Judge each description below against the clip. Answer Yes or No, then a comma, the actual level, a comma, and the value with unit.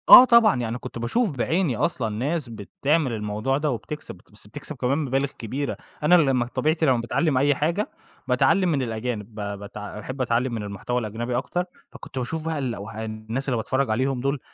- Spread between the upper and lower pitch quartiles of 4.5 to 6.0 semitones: Yes, average, 5.0 semitones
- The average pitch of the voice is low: Yes, low, 130 Hz